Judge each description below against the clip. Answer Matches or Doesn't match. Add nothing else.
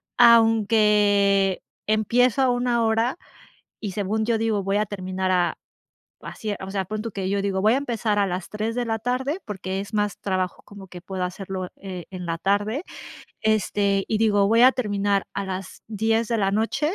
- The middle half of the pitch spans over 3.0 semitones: Doesn't match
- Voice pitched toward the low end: Doesn't match